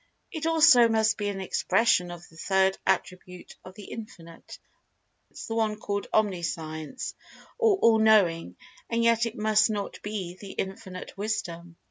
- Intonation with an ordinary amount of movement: Yes, average, 3.8 semitones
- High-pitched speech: Yes, high, 205 Hz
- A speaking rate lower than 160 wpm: Yes, slow, 135 wpm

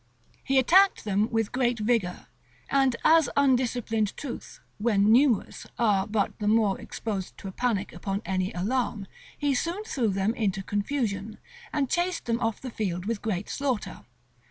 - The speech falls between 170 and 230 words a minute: No, average, 155 wpm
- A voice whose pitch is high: Yes, high, 225 Hz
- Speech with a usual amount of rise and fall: Yes, average, 4.5 semitones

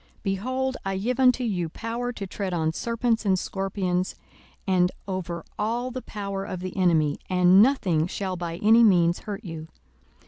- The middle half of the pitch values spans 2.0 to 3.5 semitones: No, average, 4.3 semitones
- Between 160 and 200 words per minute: Yes, average, 170 wpm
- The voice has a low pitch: No, high, 195 Hz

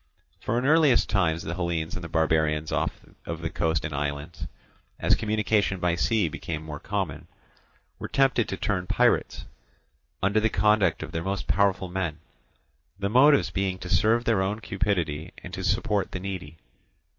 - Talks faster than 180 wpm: No, average, 165 wpm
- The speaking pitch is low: Yes, very low, 95 Hz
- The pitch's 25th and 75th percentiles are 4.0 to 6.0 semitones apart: Yes, average, 4.3 semitones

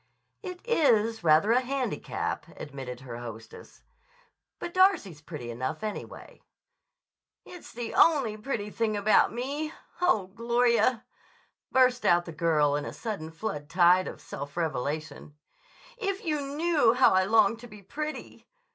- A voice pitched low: No, high, 215 Hz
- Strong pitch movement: Yes, wide, 8.7 semitones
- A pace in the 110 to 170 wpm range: Yes, average, 140 wpm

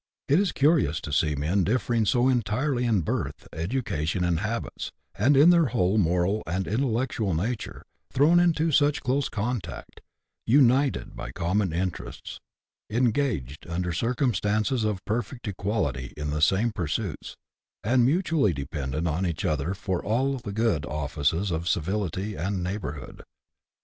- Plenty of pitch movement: Yes, wide, 6.6 semitones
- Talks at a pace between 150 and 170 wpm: No, average, 140 wpm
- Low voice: Yes, low, 105 Hz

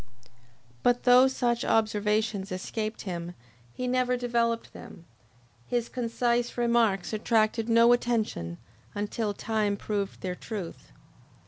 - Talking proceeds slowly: Yes, slow, 110 wpm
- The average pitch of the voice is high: Yes, high, 225 Hz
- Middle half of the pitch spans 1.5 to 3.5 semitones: Yes, average, 2.7 semitones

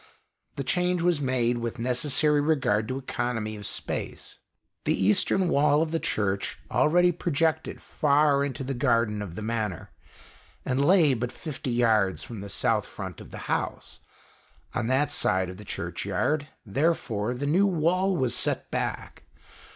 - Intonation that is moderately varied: No, wide, 6.1 semitones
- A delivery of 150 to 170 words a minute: Yes, average, 155 wpm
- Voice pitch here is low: Yes, low, 130 Hz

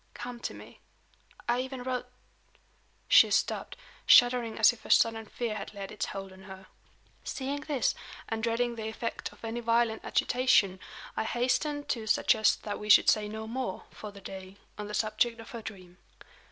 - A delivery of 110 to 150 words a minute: No, average, 180 wpm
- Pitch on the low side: No, high, 225 Hz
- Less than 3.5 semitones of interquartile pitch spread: Yes, narrow, 2.5 semitones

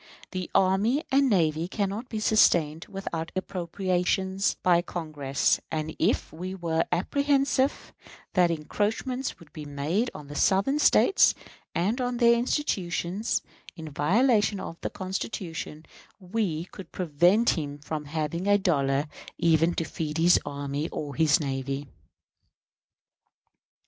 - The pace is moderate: No, slow, 125 wpm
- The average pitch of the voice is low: No, medium, 175 Hz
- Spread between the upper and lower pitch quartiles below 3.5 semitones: No, average, 4.9 semitones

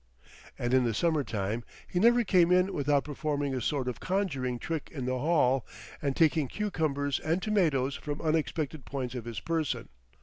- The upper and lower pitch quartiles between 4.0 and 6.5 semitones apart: Yes, average, 4.4 semitones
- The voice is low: No, medium, 145 Hz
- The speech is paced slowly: No, average, 175 wpm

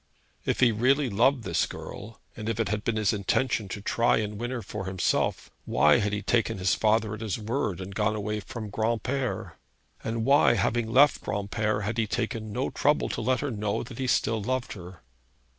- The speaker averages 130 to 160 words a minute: No, fast, 205 wpm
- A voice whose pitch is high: No, low, 110 Hz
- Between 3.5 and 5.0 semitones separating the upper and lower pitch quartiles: No, narrow, 2.5 semitones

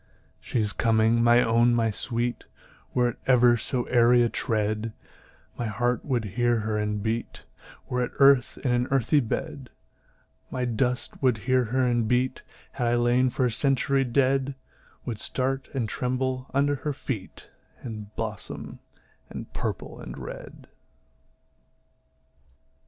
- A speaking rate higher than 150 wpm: No, average, 145 wpm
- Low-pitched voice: Yes, low, 120 Hz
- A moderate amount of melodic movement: No, narrow, 2.2 semitones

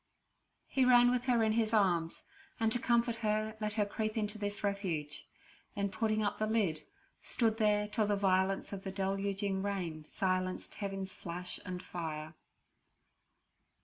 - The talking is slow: No, average, 155 wpm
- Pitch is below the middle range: No, high, 205 Hz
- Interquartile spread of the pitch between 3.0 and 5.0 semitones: No, narrow, 2.5 semitones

